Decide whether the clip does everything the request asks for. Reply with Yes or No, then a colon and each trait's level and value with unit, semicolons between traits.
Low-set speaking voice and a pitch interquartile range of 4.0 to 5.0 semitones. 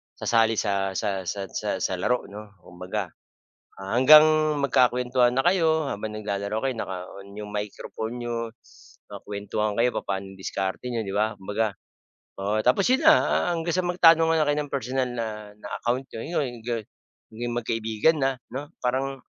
Yes: low, 115 Hz; average, 4.6 semitones